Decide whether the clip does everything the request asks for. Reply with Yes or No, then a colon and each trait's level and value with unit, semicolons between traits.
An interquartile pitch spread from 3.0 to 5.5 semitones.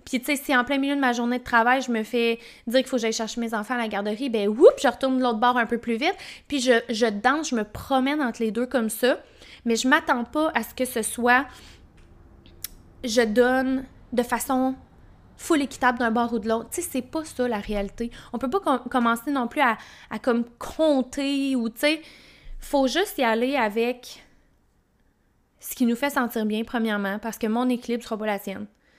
No: narrow, 2.6 semitones